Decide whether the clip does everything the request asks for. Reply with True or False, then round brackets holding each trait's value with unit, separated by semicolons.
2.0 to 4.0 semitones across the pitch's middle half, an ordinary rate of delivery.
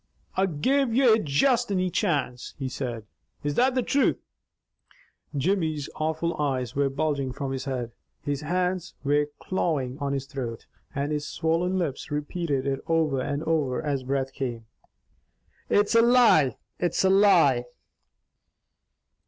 False (5.1 semitones; 145 wpm)